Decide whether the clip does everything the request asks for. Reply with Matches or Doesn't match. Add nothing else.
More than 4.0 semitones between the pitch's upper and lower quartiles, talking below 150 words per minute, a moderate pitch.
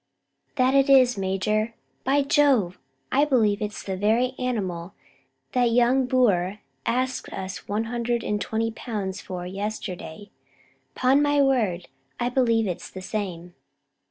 Doesn't match